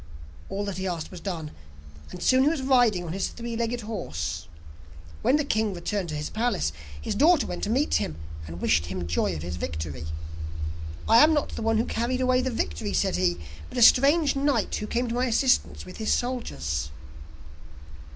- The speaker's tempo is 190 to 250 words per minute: Yes, average, 200 wpm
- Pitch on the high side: Yes, high, 215 Hz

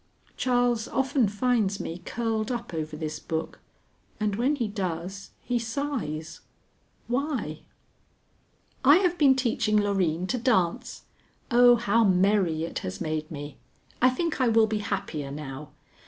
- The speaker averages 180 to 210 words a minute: No, average, 140 wpm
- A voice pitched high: Yes, high, 210 Hz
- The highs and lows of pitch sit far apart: Yes, wide, 7.0 semitones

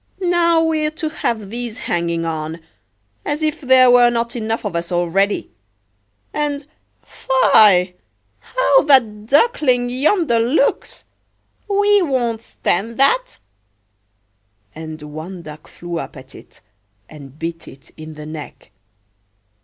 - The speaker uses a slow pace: Yes, slow, 115 wpm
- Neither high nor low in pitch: No, high, 230 Hz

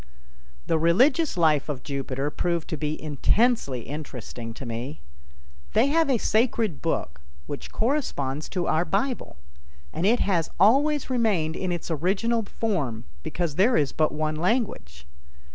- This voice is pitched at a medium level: Yes, medium, 165 Hz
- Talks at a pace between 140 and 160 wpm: Yes, average, 145 wpm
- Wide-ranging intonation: Yes, wide, 7.7 semitones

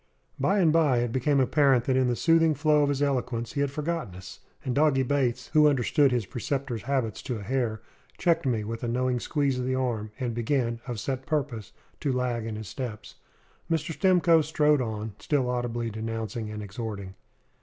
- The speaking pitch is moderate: No, low, 130 Hz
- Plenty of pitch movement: No, average, 3.9 semitones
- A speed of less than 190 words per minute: No, average, 195 wpm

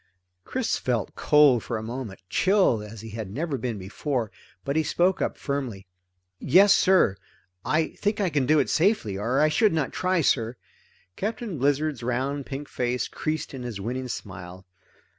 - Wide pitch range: Yes, wide, 5.8 semitones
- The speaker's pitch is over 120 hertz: Yes, low, 135 Hz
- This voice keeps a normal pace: Yes, average, 170 wpm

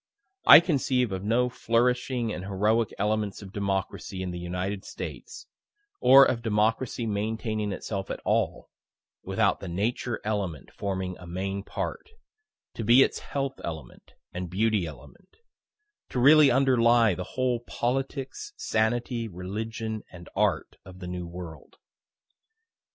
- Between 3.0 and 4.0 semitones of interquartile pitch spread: No, average, 4.4 semitones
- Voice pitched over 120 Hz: No, low, 110 Hz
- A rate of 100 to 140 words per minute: Yes, slow, 135 wpm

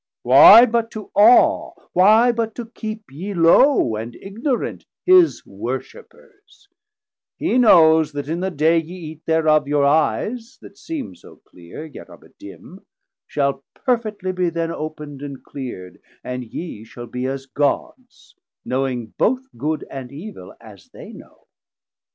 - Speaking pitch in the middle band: Yes, medium, 165 Hz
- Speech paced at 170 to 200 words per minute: No, average, 145 wpm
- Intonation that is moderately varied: No, wide, 8.3 semitones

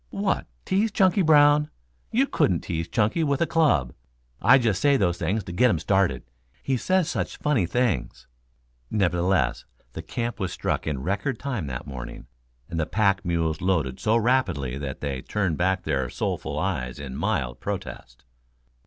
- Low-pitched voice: Yes, very low, 95 Hz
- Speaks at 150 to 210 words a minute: Yes, average, 165 wpm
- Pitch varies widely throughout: Yes, wide, 8.5 semitones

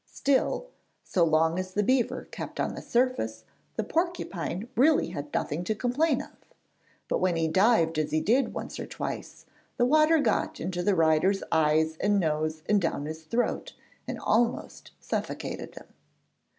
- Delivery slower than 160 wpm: No, average, 165 wpm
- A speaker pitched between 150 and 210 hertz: Yes, medium, 185 Hz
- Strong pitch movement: Yes, wide, 7.4 semitones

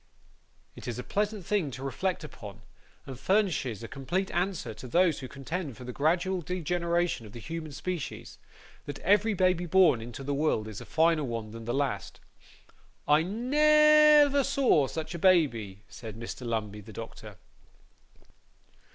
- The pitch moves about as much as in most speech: No, wide, 7.5 semitones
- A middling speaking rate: Yes, average, 160 wpm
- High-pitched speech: No, medium, 155 Hz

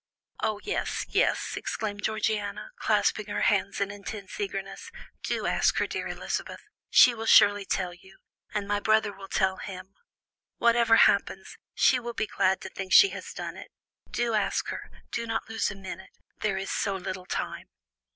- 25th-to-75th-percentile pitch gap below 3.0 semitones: Yes, narrow, 2.4 semitones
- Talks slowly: No, average, 170 wpm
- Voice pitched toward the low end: No, high, 205 Hz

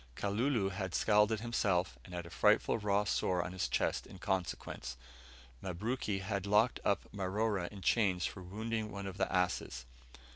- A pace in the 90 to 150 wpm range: No, average, 160 wpm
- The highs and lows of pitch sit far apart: No, average, 2.7 semitones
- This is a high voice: No, low, 100 Hz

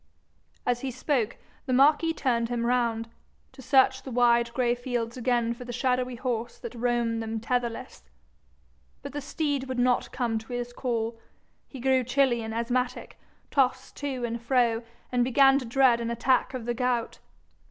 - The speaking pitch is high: Yes, high, 245 Hz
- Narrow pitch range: Yes, narrow, 1.7 semitones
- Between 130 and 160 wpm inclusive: No, average, 170 wpm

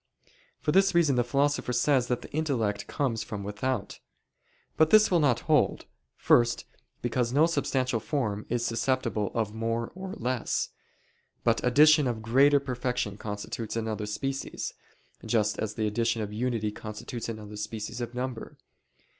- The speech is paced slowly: No, average, 145 wpm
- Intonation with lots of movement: No, average, 3.8 semitones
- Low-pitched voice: Yes, low, 120 Hz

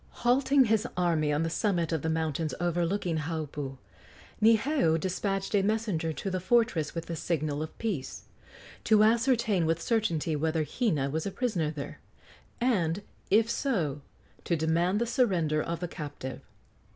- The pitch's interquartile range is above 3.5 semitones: Yes, wide, 5.5 semitones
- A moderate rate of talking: Yes, average, 150 wpm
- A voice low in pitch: No, medium, 170 Hz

